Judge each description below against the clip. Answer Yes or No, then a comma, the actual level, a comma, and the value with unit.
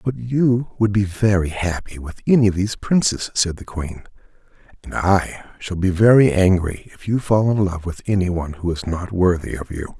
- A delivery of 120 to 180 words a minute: No, average, 200 wpm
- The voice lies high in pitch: No, very low, 95 Hz